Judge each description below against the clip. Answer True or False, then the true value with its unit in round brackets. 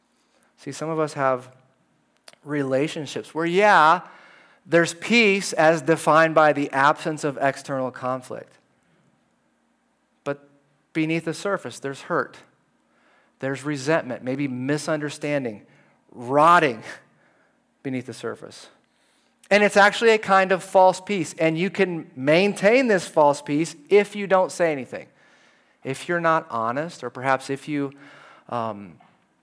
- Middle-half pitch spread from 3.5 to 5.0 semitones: True (3.9 semitones)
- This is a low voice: False (155 Hz)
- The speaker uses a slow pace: True (125 wpm)